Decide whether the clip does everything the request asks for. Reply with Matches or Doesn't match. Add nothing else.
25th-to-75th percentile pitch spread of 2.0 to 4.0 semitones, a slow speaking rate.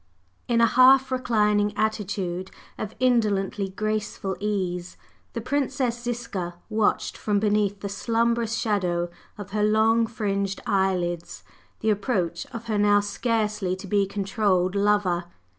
Matches